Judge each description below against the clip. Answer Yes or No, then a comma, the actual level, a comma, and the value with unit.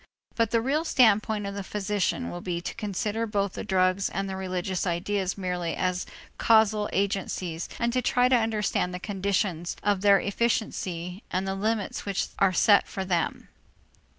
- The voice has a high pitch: Yes, high, 200 Hz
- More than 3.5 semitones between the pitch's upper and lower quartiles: No, narrow, 2.6 semitones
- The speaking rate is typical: Yes, average, 170 wpm